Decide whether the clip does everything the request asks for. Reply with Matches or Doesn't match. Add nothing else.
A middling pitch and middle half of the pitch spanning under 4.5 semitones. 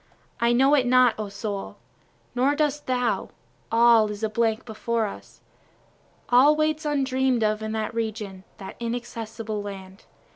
Doesn't match